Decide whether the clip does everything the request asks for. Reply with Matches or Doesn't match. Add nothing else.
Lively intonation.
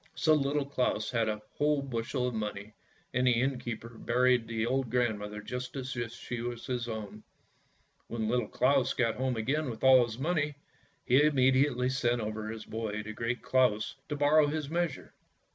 Doesn't match